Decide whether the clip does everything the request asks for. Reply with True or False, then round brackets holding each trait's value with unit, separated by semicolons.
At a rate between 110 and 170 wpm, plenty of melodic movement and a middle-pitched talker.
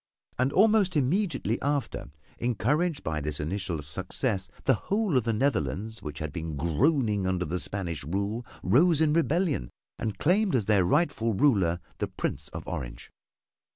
False (155 wpm; 8.9 semitones; 110 Hz)